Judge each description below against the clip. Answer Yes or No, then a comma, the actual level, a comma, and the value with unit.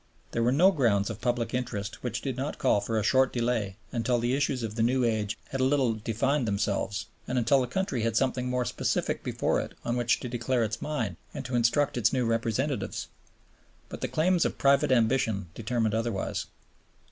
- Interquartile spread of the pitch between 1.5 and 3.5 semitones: Yes, average, 2.7 semitones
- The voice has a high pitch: No, low, 120 Hz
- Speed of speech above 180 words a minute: Yes, average, 200 wpm